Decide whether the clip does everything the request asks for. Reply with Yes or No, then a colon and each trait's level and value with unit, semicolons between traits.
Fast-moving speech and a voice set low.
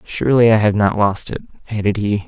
Yes: fast, 210 wpm; low, 105 Hz